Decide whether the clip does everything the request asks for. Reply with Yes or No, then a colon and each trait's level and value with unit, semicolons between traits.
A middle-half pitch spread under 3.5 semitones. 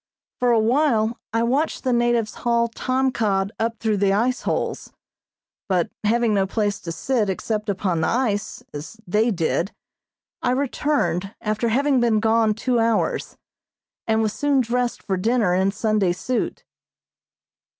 Yes: average, 3.1 semitones